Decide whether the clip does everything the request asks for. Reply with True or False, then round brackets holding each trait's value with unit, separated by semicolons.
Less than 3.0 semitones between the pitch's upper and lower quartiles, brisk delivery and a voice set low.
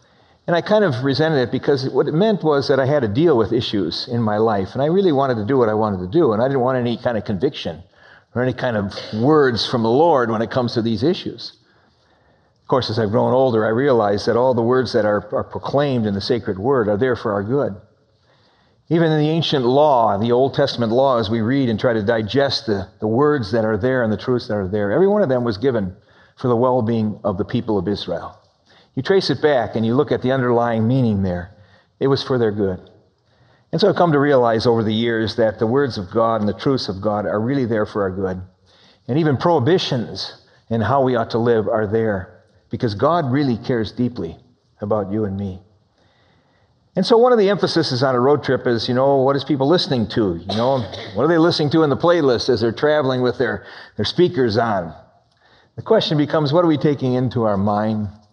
False (4.4 semitones; 235 wpm; 120 Hz)